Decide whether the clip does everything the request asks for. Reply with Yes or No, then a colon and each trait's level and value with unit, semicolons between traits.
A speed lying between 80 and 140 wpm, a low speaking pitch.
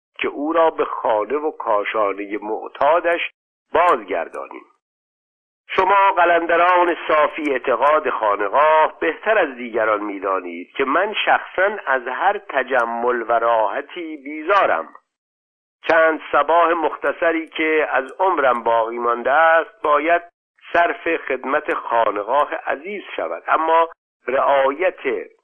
No: slow, 105 wpm; medium, 160 Hz